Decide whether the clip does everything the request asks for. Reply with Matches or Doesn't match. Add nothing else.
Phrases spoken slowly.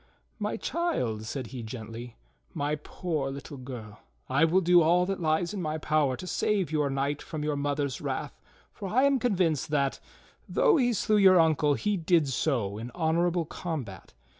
Doesn't match